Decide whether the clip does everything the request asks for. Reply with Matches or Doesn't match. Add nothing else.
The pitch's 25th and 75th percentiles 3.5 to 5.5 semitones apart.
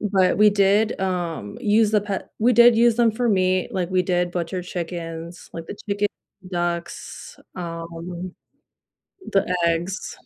Doesn't match